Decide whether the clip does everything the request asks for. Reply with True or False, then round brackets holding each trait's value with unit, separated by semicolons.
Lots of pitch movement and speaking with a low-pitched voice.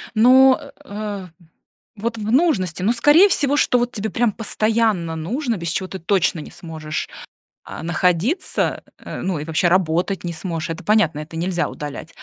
False (5.7 semitones; 190 Hz)